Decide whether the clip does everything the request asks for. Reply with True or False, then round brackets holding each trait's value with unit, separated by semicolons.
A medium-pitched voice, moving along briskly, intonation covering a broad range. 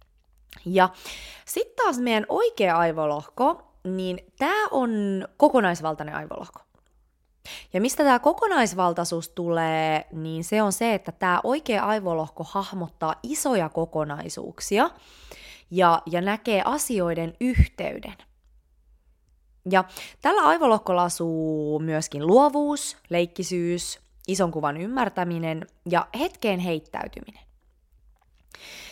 False (180 Hz; 95 wpm; 5.8 semitones)